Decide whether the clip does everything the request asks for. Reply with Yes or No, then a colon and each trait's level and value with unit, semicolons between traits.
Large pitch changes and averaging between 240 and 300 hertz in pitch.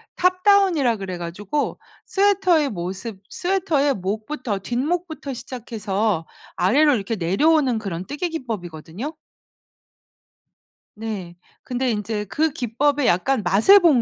Yes: wide, 7.6 semitones; high, 245 Hz